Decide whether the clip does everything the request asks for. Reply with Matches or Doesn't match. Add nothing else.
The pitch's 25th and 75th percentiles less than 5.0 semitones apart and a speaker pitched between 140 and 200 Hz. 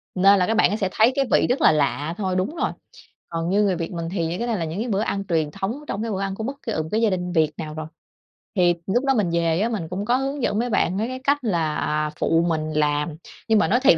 Doesn't match